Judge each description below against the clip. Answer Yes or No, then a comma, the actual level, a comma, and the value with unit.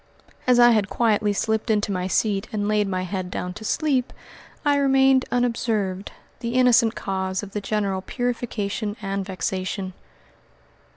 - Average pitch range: Yes, average, 3.7 semitones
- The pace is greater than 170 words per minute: No, average, 150 wpm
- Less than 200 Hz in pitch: No, high, 210 Hz